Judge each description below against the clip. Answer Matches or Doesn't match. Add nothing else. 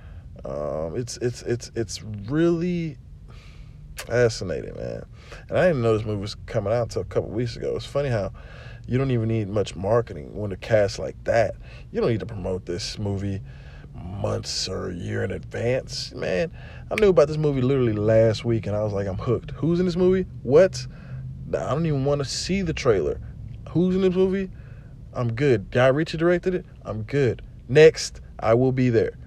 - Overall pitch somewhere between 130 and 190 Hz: Doesn't match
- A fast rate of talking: Doesn't match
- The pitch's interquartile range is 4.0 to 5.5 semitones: Matches